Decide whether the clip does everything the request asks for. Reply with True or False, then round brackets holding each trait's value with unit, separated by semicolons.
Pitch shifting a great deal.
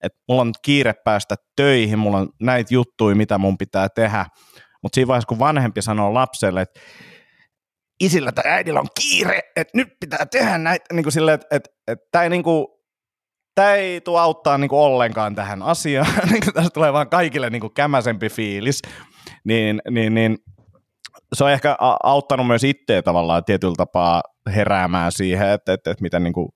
True (6.1 semitones)